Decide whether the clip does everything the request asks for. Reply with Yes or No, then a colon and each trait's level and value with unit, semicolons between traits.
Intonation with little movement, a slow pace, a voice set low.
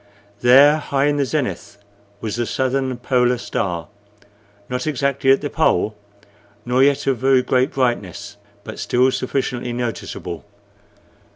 Yes: narrow, 2.1 semitones; slow, 130 wpm; low, 125 Hz